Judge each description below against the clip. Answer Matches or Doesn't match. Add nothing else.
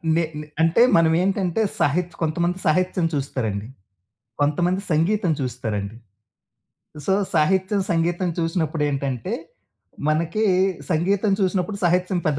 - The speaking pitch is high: Doesn't match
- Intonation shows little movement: Doesn't match